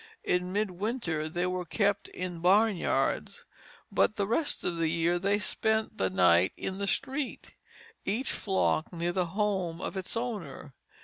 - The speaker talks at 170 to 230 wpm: No, average, 150 wpm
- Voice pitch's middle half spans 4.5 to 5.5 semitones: No, average, 3.6 semitones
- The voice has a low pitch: No, medium, 185 Hz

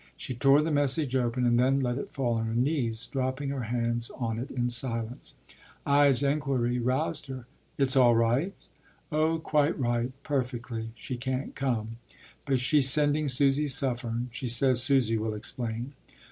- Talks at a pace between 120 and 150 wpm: No, average, 160 wpm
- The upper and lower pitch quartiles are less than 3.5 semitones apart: Yes, average, 2.8 semitones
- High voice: No, low, 130 Hz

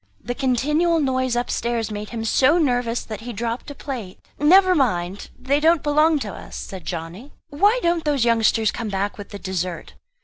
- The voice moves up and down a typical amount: No, wide, 5.8 semitones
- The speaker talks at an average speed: Yes, average, 180 wpm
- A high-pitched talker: Yes, high, 245 Hz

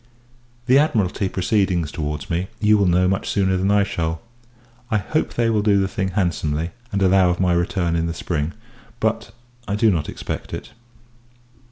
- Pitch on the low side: Yes, very low, 95 Hz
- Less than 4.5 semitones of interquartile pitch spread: Yes, average, 3.0 semitones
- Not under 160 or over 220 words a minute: Yes, average, 180 wpm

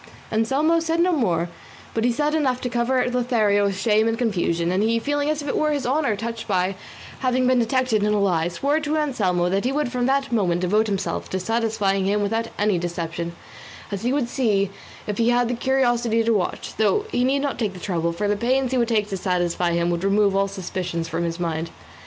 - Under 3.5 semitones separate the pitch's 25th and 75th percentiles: No, average, 5.2 semitones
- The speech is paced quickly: Yes, fast, 225 wpm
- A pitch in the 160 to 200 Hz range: No, high, 220 Hz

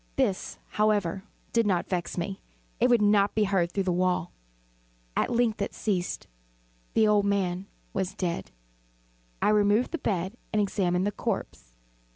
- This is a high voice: Yes, high, 200 Hz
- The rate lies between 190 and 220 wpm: No, average, 155 wpm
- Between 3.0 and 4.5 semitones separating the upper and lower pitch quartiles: No, narrow, 2.6 semitones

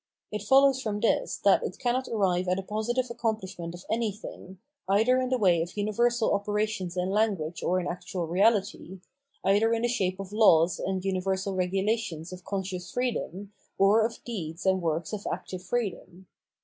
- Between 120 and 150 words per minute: No, average, 170 wpm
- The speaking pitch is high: Yes, high, 195 Hz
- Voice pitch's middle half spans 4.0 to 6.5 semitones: No, average, 3.6 semitones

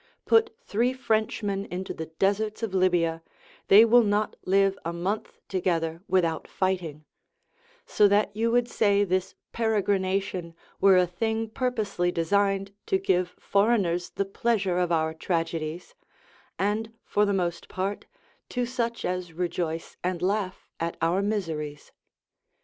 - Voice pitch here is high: Yes, high, 195 Hz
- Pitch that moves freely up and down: No, average, 3.4 semitones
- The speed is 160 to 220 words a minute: No, slow, 135 wpm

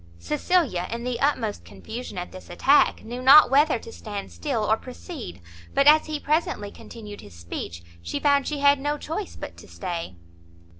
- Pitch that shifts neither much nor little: No, wide, 6.9 semitones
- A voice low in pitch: No, high, 245 Hz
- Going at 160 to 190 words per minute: Yes, average, 180 wpm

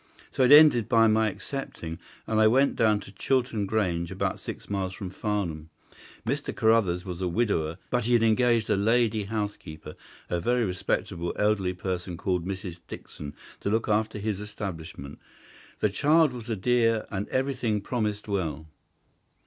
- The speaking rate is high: No, average, 160 wpm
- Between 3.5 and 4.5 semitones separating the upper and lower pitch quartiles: Yes, average, 3.9 semitones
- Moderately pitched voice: No, low, 105 Hz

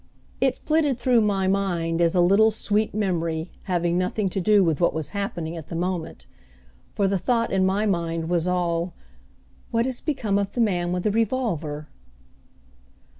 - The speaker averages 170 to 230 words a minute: Yes, average, 175 wpm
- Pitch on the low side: No, high, 190 Hz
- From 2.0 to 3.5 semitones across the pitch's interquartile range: No, average, 3.9 semitones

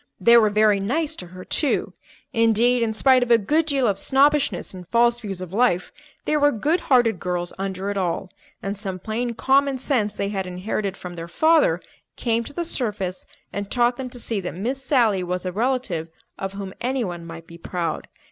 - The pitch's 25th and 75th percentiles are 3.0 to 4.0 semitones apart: No, average, 5.3 semitones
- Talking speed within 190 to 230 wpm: Yes, average, 200 wpm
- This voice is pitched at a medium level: No, high, 215 Hz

